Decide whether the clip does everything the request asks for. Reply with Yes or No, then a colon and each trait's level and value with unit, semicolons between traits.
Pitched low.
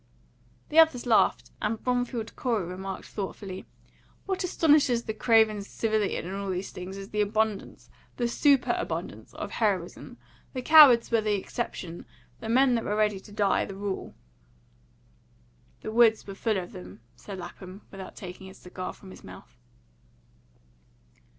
No: high, 210 Hz